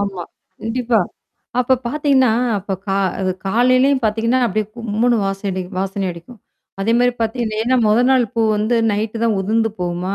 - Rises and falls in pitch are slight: No, average, 3.7 semitones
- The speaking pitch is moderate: No, high, 225 Hz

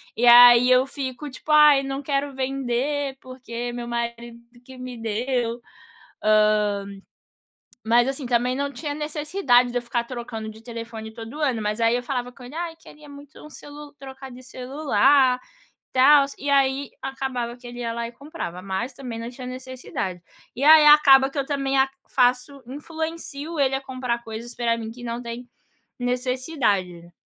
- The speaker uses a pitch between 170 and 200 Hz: No, very high, 255 Hz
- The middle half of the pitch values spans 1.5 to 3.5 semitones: Yes, average, 2.7 semitones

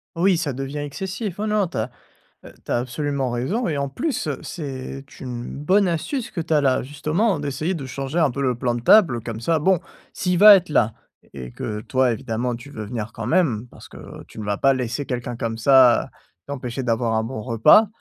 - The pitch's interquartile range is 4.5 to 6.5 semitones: Yes, wide, 5.6 semitones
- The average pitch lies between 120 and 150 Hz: Yes, low, 135 Hz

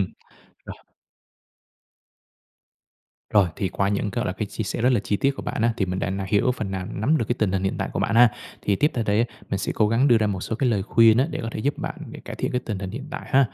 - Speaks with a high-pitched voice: No, low, 110 Hz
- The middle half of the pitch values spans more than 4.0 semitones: No, average, 3.7 semitones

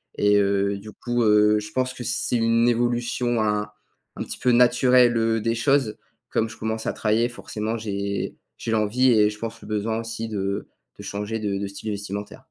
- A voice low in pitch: Yes, low, 110 Hz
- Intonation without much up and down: Yes, narrow, 2.2 semitones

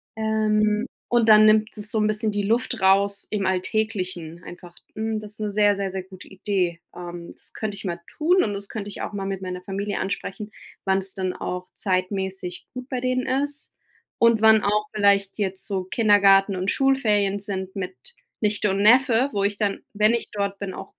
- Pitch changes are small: Yes, narrow, 2.1 semitones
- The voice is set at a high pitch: Yes, high, 205 Hz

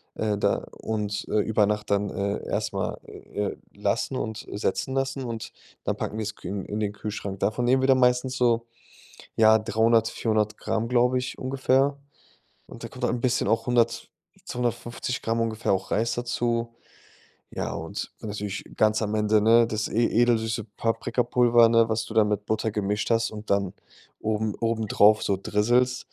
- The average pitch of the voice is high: No, low, 110 Hz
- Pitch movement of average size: No, narrow, 2.2 semitones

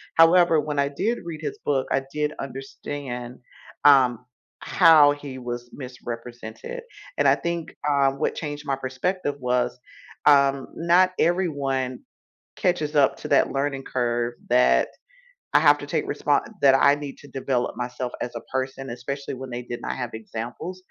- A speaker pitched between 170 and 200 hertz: No, low, 135 Hz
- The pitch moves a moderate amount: Yes, average, 3.2 semitones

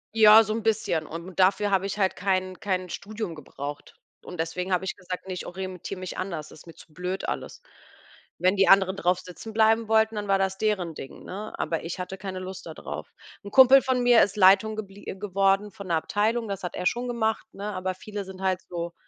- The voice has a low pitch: No, high, 190 Hz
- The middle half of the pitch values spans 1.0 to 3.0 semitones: Yes, narrow, 2.6 semitones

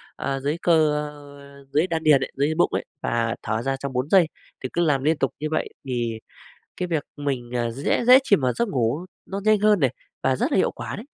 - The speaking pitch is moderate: Yes, medium, 145 Hz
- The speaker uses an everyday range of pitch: Yes, average, 4.6 semitones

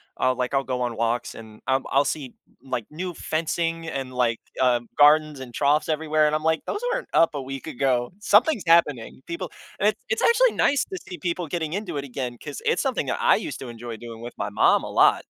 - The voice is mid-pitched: Yes, medium, 145 Hz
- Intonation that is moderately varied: Yes, average, 4.9 semitones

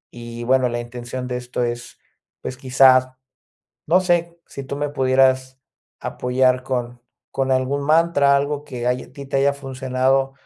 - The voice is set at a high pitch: No, low, 130 Hz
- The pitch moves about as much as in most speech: No, narrow, 2.0 semitones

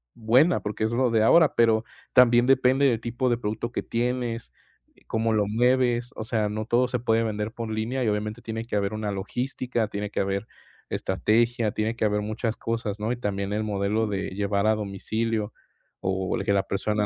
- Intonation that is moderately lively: No, narrow, 2.3 semitones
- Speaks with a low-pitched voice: Yes, low, 110 Hz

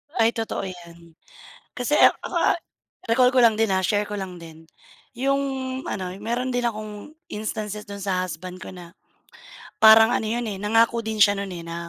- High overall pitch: Yes, high, 210 Hz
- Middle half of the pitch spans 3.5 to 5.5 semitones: Yes, average, 3.8 semitones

